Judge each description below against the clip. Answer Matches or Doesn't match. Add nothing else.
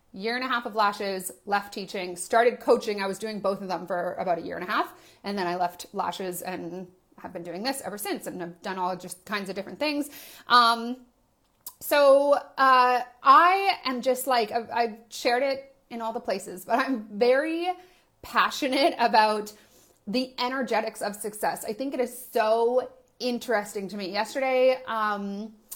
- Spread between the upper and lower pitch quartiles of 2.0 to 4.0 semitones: Doesn't match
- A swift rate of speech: Doesn't match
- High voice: Matches